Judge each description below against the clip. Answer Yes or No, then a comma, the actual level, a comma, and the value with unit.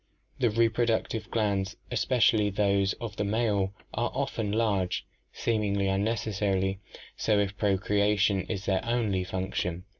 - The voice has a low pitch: Yes, low, 105 Hz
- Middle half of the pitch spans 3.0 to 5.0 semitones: No, narrow, 2.4 semitones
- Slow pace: Yes, slow, 125 wpm